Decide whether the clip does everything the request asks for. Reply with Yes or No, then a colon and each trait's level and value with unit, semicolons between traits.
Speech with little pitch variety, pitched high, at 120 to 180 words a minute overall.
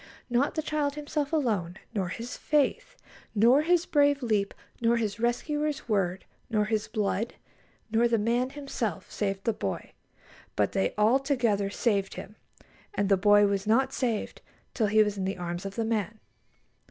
No: average, 5.0 semitones; high, 225 Hz; average, 165 wpm